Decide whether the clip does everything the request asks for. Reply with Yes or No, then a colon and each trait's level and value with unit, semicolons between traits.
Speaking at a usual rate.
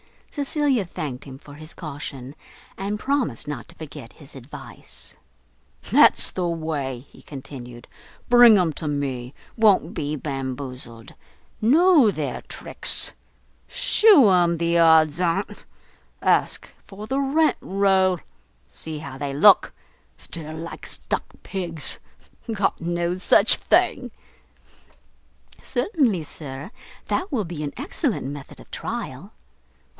No: slow, 120 wpm